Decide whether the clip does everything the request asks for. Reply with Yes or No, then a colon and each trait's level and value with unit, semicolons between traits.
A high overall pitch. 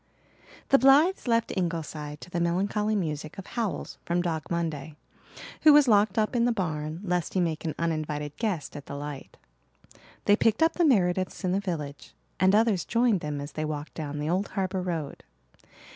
No: medium, 175 Hz